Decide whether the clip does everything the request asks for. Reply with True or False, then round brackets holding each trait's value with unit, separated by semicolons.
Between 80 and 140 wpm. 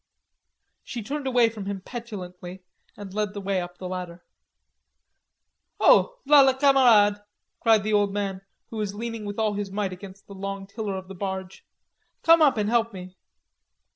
False (170 wpm)